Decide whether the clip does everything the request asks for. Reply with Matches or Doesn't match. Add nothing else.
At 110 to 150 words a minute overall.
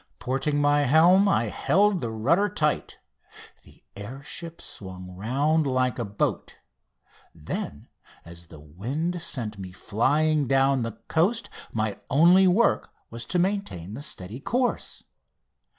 Matches